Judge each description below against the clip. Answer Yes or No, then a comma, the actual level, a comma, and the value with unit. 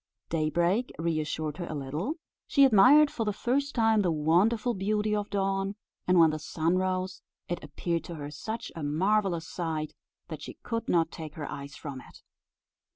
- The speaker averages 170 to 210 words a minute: Yes, average, 175 wpm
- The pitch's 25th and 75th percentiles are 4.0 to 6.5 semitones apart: Yes, average, 5.1 semitones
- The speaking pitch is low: No, medium, 180 Hz